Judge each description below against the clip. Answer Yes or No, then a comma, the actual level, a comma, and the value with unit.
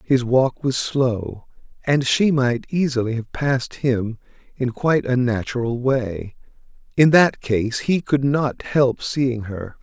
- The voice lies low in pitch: Yes, low, 125 Hz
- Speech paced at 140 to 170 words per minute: Yes, average, 155 wpm